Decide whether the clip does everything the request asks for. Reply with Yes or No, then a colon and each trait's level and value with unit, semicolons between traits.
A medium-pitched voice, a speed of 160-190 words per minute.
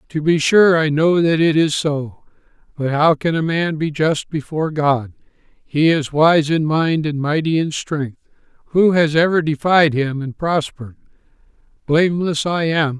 Yes: medium, 155 Hz; average, 170 wpm